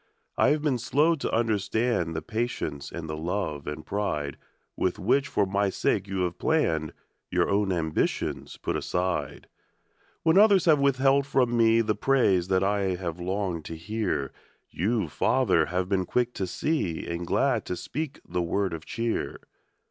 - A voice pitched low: Yes, low, 100 Hz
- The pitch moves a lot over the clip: Yes, wide, 5.9 semitones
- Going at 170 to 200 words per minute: No, average, 150 wpm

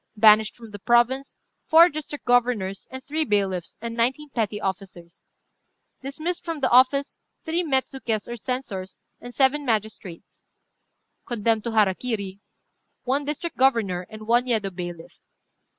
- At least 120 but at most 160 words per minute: Yes, slow, 135 wpm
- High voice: Yes, high, 235 Hz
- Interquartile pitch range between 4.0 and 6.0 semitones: Yes, average, 4.7 semitones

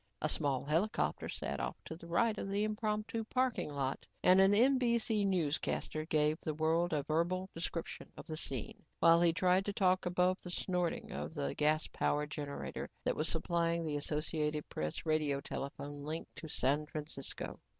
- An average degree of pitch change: Yes, average, 3.7 semitones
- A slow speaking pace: No, average, 170 wpm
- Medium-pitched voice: Yes, medium, 165 Hz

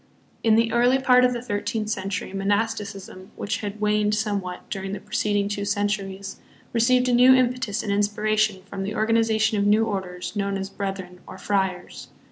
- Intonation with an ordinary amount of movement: No, narrow, 2.2 semitones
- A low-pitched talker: No, high, 205 Hz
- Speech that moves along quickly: No, average, 180 wpm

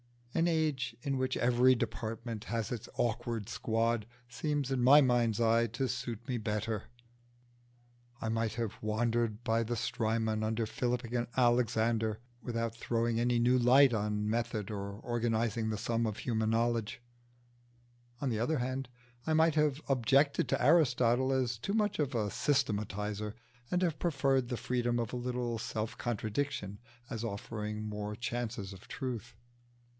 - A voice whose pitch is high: No, low, 120 Hz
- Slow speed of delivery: No, average, 150 wpm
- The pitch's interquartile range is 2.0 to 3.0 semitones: Yes, narrow, 2.4 semitones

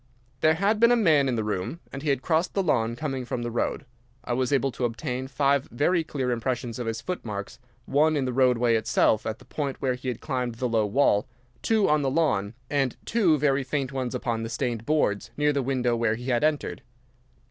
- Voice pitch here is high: No, low, 130 Hz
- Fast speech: Yes, fast, 225 wpm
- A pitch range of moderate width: Yes, average, 3.8 semitones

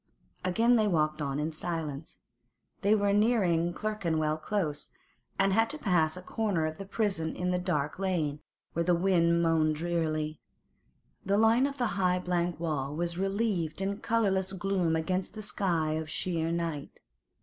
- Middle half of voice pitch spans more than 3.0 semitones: Yes, average, 3.7 semitones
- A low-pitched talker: No, medium, 175 Hz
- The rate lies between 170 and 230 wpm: No, average, 160 wpm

